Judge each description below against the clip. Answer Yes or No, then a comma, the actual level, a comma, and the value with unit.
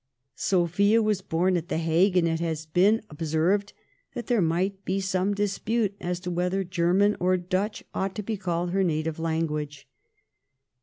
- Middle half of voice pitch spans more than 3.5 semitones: No, average, 3.2 semitones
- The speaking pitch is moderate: Yes, medium, 180 Hz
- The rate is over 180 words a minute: No, average, 165 wpm